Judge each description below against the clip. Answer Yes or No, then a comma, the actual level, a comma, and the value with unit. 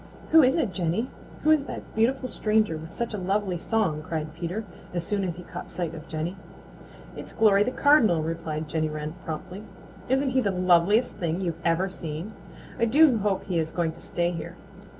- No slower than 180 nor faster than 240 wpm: Yes, average, 195 wpm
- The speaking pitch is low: No, medium, 185 Hz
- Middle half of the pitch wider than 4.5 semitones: Yes, average, 5.0 semitones